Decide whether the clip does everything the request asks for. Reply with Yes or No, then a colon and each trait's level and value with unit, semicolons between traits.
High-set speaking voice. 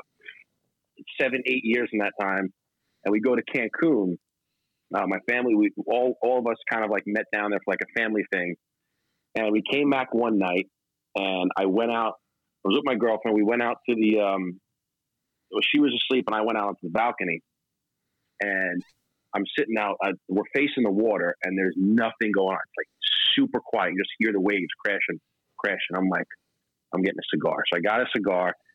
No: low, 110 Hz